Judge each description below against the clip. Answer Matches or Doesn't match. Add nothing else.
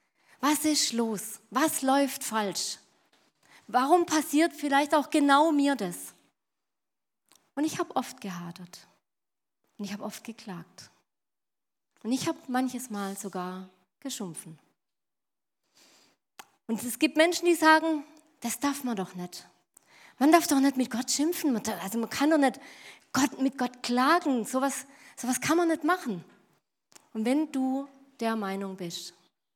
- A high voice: Matches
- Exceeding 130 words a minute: Matches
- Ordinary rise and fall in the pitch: Doesn't match